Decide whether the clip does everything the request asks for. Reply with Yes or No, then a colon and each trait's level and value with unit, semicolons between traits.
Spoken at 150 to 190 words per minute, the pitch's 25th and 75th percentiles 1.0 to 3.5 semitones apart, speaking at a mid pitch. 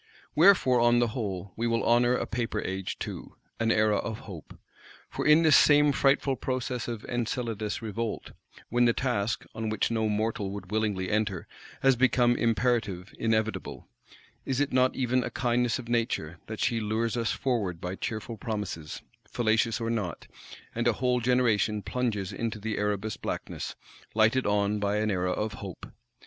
No: average, 165 wpm; average, 2.8 semitones; low, 115 Hz